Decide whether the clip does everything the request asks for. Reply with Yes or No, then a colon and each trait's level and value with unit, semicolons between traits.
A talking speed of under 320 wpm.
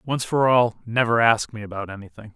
Yes: fast, 205 wpm